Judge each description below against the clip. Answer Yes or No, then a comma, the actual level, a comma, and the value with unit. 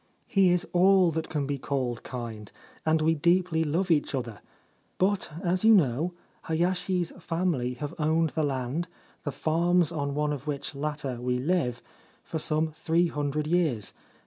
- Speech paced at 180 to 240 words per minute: No, average, 160 wpm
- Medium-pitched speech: Yes, medium, 155 Hz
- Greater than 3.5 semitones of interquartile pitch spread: Yes, average, 3.9 semitones